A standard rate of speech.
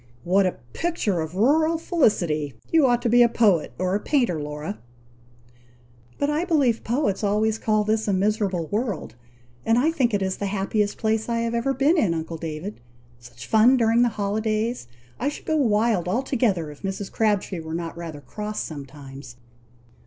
Yes: average, 175 wpm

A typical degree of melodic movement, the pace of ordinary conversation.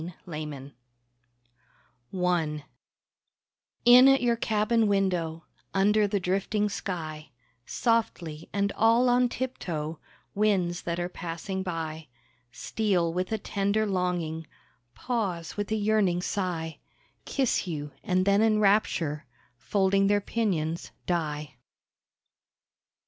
No: average, 4.4 semitones; slow, 110 wpm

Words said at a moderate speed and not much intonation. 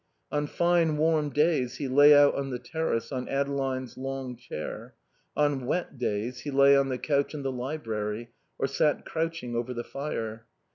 No: average, 175 wpm; average, 3.0 semitones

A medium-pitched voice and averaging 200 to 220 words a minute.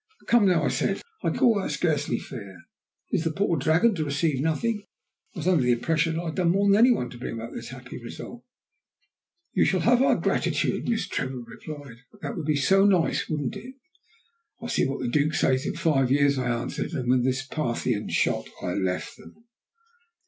Yes: medium, 150 Hz; fast, 205 wpm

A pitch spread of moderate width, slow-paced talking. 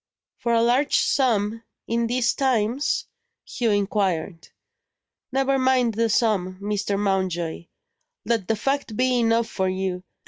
Yes: average, 3.9 semitones; slow, 130 wpm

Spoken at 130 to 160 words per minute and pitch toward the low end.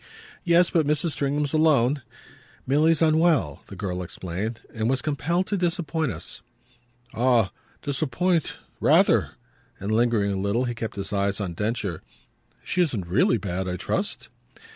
Yes: average, 140 wpm; low, 120 Hz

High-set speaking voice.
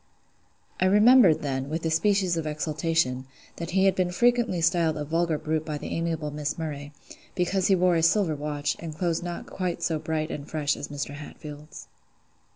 No: medium, 160 Hz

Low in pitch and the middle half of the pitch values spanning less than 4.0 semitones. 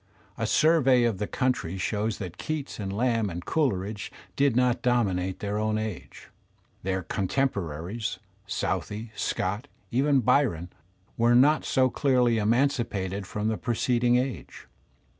No: low, 115 Hz; average, 4.4 semitones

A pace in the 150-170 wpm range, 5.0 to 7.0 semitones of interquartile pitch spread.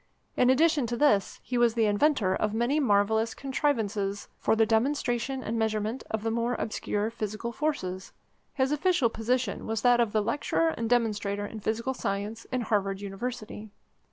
No: average, 160 wpm; average, 3.2 semitones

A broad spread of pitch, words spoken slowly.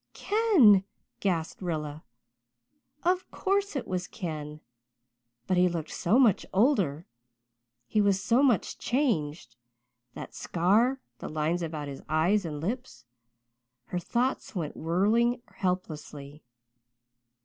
Yes: wide, 7.2 semitones; slow, 115 wpm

